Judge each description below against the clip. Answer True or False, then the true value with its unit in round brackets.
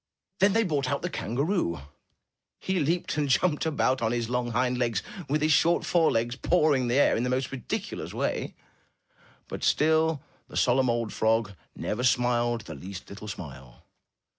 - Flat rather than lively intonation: False (4.7 semitones)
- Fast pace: False (165 wpm)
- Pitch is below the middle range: True (125 Hz)